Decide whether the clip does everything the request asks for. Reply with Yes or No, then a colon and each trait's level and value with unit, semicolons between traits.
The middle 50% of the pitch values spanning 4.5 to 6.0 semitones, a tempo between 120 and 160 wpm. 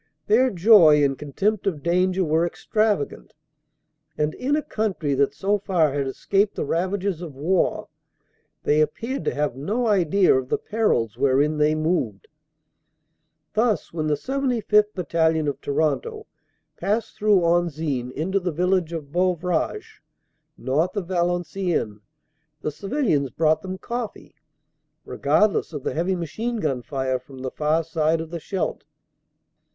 Yes: average, 5.1 semitones; average, 145 wpm